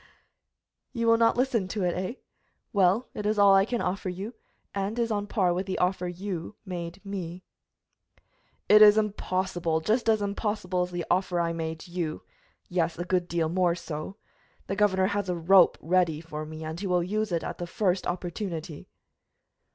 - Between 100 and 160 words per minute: No, average, 185 wpm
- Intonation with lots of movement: No, average, 2.9 semitones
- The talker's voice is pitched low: No, medium, 185 Hz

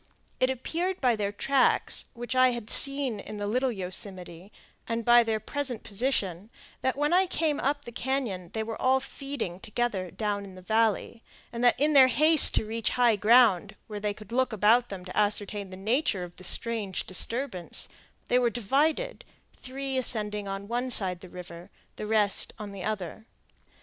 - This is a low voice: No, high, 225 Hz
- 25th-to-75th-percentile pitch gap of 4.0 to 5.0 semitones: Yes, average, 4.3 semitones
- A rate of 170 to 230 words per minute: Yes, average, 180 wpm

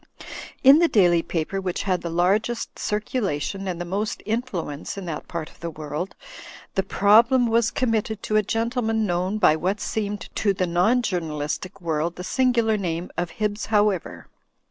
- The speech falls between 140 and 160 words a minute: No, average, 170 wpm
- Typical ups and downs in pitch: Yes, average, 4.1 semitones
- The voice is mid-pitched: No, high, 195 Hz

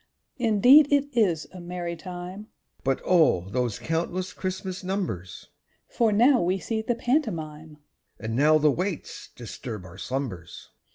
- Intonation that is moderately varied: No, wide, 6.5 semitones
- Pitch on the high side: No, medium, 175 Hz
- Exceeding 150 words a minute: No, average, 145 wpm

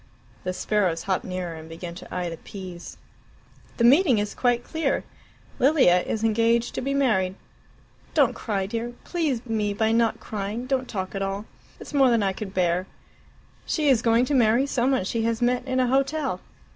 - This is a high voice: Yes, high, 225 Hz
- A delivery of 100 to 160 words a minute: No, average, 185 wpm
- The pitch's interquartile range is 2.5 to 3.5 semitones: No, average, 5.0 semitones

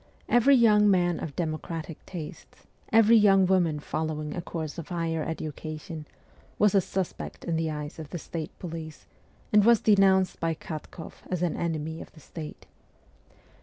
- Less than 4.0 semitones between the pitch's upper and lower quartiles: Yes, average, 3.4 semitones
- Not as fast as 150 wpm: No, average, 160 wpm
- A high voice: No, medium, 165 Hz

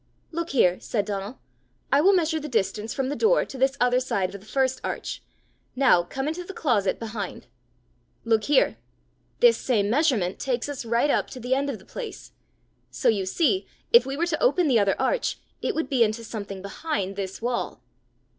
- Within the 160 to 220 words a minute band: Yes, average, 195 wpm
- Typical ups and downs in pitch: No, wide, 6.4 semitones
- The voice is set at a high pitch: Yes, very high, 255 Hz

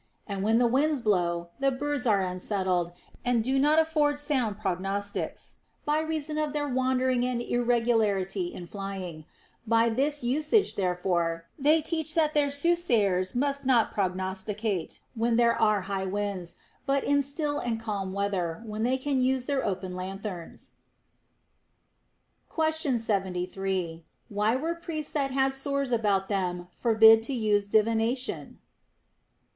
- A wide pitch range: Yes, wide, 6.3 semitones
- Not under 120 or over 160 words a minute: Yes, average, 140 wpm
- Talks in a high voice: Yes, high, 225 Hz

